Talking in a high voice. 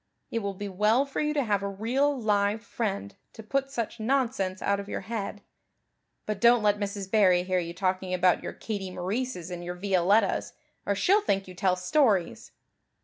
Yes: high, 200 Hz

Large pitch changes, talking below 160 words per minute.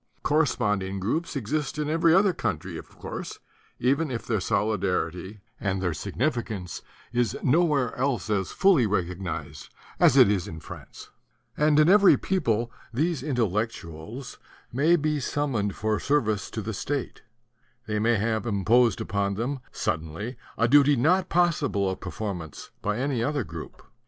Yes: wide, 6.7 semitones; average, 150 wpm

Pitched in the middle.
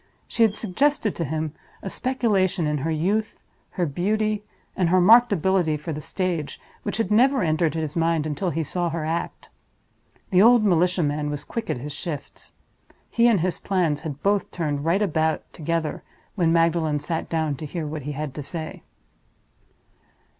Yes: medium, 170 Hz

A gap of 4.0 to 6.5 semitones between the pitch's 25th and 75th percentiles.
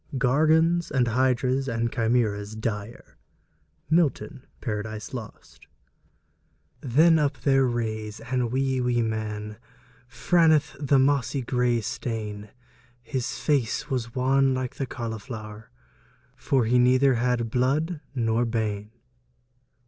No: average, 3.2 semitones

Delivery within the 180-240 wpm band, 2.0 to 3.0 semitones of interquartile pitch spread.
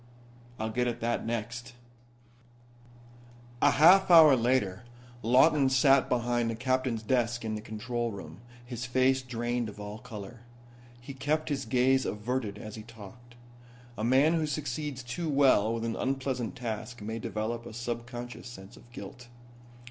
No: average, 150 wpm; average, 2.7 semitones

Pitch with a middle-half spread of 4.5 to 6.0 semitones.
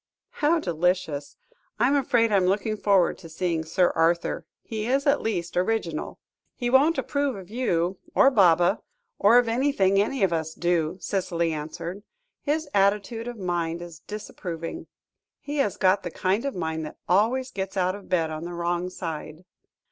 Yes: average, 5.0 semitones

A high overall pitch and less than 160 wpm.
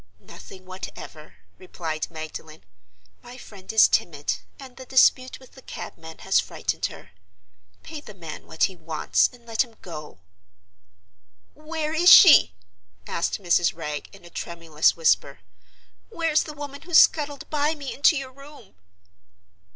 Yes: high, 220 Hz; average, 145 wpm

